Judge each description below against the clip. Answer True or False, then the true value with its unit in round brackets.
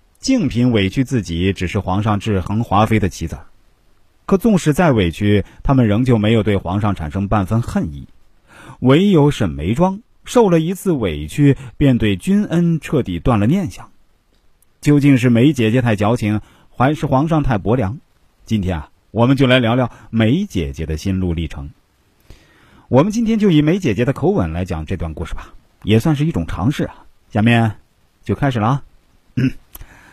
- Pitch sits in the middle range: False (110 Hz)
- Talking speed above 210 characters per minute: True (250 characters per minute)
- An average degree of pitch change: False (6.8 semitones)